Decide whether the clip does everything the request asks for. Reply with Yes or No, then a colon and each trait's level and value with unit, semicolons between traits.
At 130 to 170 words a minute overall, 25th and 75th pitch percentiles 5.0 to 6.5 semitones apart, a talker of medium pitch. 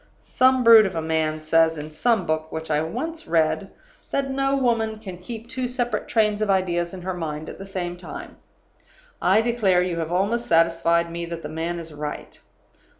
No: average, 195 wpm; wide, 5.6 semitones; medium, 180 Hz